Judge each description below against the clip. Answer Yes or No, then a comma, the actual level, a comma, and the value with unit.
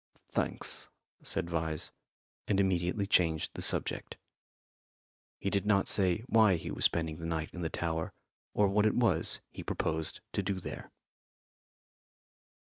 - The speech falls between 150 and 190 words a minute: No, average, 140 wpm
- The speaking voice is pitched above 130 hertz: No, very low, 90 Hz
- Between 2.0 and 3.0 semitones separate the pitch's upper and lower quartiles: No, average, 3.5 semitones